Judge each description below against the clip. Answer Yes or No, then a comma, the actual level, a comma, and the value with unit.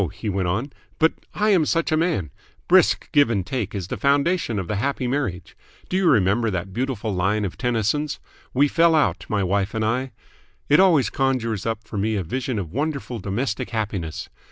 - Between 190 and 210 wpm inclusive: Yes, average, 195 wpm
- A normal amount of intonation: No, wide, 6.0 semitones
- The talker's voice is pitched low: Yes, low, 115 Hz